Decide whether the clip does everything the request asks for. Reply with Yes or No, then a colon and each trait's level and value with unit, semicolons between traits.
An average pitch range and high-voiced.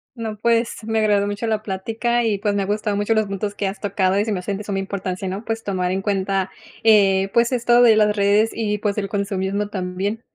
No: narrow, 2.1 semitones; high, 205 Hz